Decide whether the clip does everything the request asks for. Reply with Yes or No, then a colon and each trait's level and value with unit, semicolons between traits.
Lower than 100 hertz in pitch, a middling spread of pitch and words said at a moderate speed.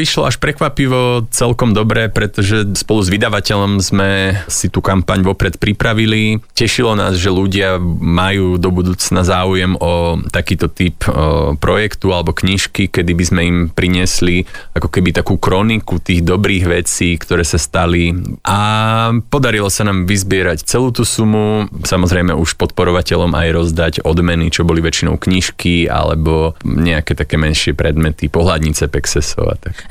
Yes: very low, 90 Hz; average, 3.3 semitones; average, 140 wpm